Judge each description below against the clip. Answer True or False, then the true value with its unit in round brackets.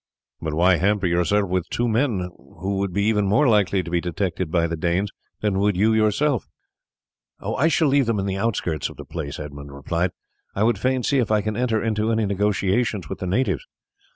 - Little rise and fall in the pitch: False (3.9 semitones)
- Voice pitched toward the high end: False (100 Hz)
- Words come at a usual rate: False (210 wpm)